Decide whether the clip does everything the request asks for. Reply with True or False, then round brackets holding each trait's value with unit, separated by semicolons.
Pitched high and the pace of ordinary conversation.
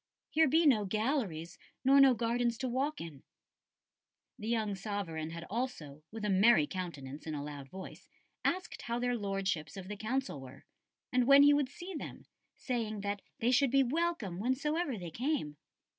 True (220 Hz; 175 wpm)